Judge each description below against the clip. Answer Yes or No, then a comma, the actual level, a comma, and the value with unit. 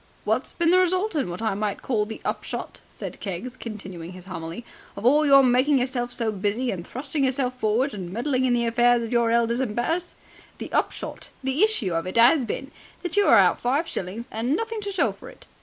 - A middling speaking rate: No, fast, 225 wpm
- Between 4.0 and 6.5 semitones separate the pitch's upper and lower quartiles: Yes, average, 4.7 semitones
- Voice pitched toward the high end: Yes, high, 245 Hz